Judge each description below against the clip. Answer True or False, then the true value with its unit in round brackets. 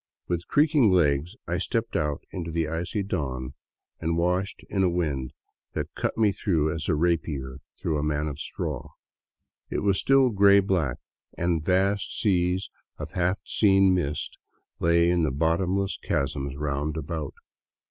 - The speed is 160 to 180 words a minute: False (150 wpm)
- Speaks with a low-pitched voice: True (85 Hz)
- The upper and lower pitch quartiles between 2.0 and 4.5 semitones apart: True (4.2 semitones)